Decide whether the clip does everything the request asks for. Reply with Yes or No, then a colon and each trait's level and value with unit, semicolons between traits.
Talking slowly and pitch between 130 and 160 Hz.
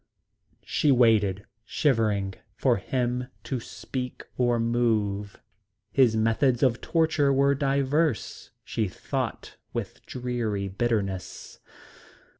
No: slow, 95 wpm; low, 120 Hz